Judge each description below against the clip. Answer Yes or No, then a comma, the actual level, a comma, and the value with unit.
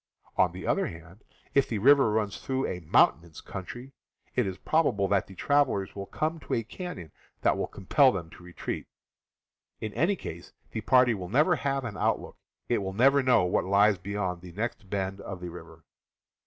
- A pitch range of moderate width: No, wide, 6.0 semitones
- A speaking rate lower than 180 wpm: No, average, 190 wpm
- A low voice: Yes, low, 105 Hz